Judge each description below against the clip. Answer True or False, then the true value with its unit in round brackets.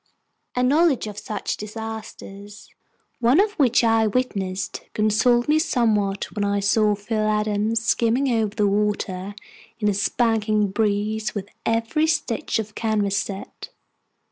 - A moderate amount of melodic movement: False (2.2 semitones)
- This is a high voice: True (215 Hz)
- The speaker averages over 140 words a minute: False (135 wpm)